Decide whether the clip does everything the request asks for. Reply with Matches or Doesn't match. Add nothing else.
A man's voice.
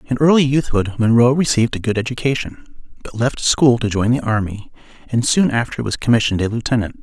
Matches